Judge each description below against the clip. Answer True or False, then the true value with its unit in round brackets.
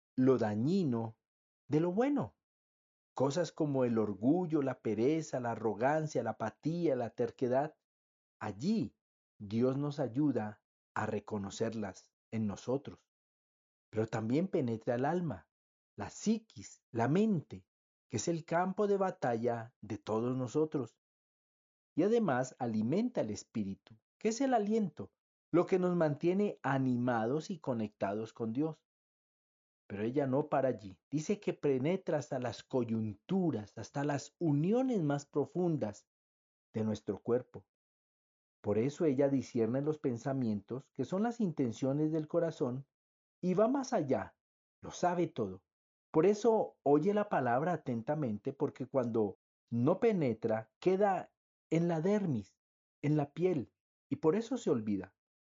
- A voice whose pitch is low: True (130 Hz)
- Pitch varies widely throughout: True (7.2 semitones)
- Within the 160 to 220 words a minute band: False (130 wpm)